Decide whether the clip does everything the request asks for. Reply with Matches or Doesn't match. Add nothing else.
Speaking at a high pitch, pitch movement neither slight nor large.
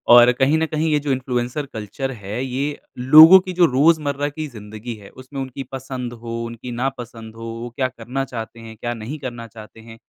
Doesn't match